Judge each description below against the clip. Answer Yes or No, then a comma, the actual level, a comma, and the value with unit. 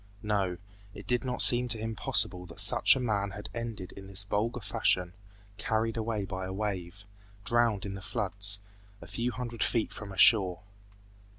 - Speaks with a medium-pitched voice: No, low, 105 Hz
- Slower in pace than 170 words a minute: No, average, 180 wpm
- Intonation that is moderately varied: Yes, average, 3.1 semitones